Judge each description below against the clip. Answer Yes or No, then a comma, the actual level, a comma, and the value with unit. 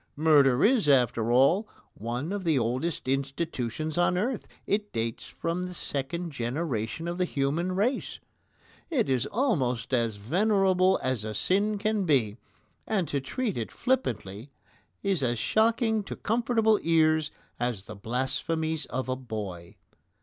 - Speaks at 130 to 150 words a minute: Yes, average, 140 wpm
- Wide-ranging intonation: Yes, wide, 7.9 semitones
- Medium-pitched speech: Yes, medium, 155 Hz